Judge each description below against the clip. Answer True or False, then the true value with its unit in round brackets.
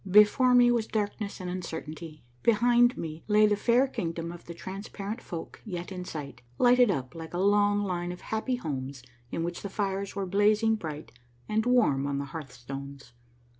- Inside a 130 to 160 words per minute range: False (175 wpm)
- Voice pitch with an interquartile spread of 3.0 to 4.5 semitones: False (4.9 semitones)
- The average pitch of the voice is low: False (190 Hz)